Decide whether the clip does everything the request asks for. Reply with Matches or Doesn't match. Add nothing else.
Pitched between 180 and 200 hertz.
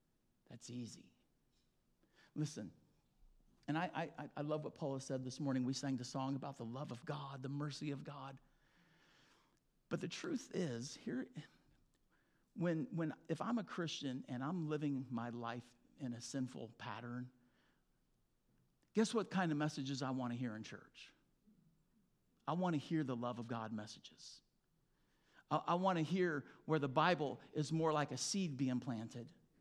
Doesn't match